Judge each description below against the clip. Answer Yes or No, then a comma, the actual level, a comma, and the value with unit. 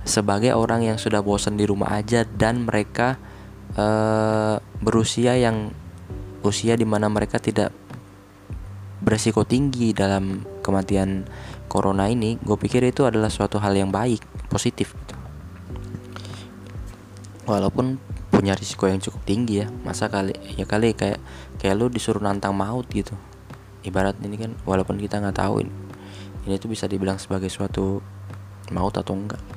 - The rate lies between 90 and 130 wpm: No, fast, 140 wpm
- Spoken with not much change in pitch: Yes, narrow, 2.0 semitones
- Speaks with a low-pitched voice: Yes, low, 100 Hz